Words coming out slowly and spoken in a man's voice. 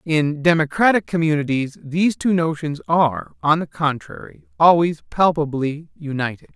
Yes: slow, 120 wpm; male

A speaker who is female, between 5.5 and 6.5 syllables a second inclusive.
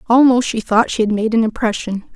Yes: female; 5.7 syllables/s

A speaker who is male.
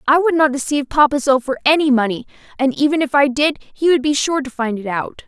No: female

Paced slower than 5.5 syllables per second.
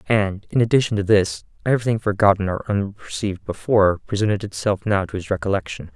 No: 6.2 syllables/s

